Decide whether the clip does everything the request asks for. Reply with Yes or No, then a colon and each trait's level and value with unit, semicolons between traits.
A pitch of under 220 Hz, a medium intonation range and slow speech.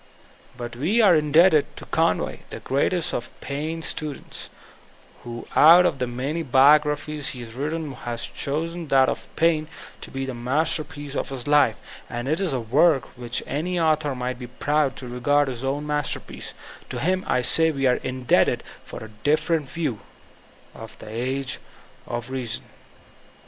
No: medium, 140 Hz; average, 3.6 semitones; average, 170 wpm